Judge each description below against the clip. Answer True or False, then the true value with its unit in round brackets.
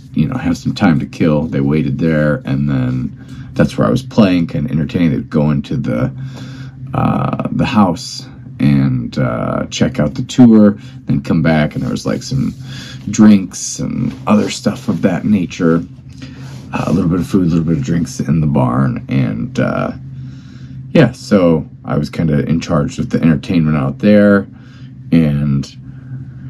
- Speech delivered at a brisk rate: False (180 wpm)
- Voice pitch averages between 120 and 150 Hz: False (105 Hz)